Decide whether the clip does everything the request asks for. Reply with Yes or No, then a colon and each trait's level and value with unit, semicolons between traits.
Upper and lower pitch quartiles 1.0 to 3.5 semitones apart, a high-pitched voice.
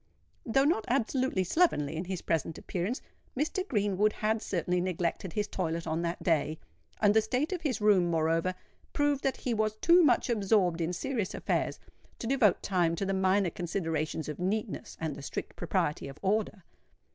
No: average, 5.0 semitones; high, 195 Hz